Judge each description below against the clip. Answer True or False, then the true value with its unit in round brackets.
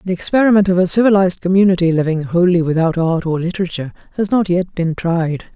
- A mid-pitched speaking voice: True (180 Hz)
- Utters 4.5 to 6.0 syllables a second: False (6.5 syllables/s)